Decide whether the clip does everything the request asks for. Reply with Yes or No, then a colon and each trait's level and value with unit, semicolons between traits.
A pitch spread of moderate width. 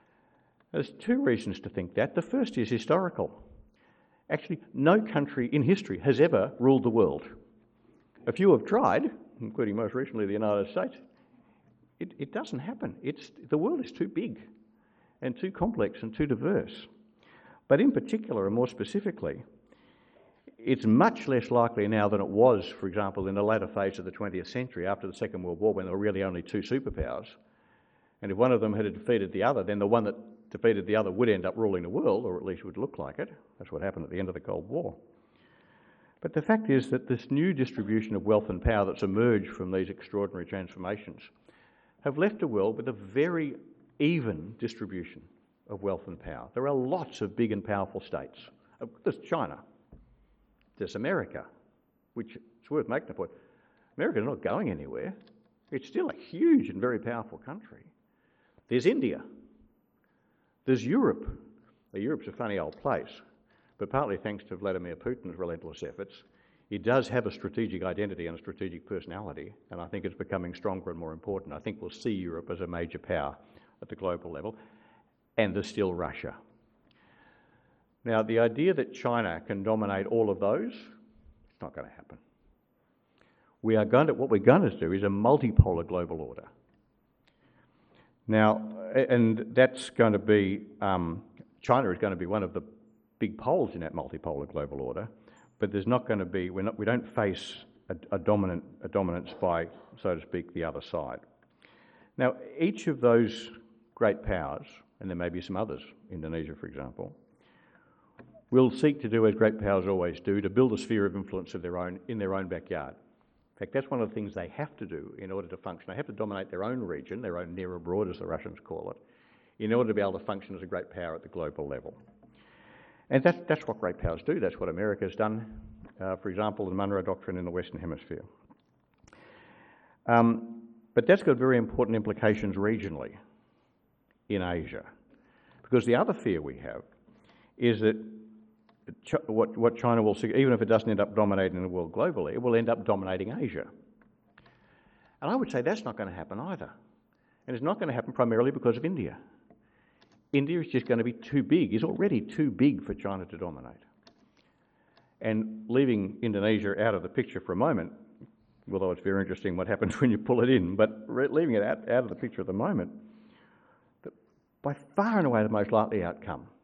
Yes: average, 4.1 semitones